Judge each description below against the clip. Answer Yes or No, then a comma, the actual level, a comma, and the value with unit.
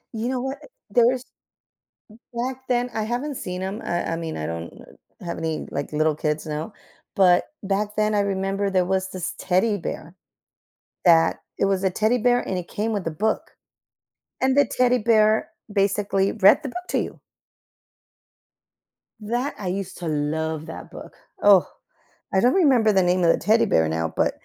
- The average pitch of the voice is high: Yes, high, 195 Hz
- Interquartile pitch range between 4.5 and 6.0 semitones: Yes, average, 5.1 semitones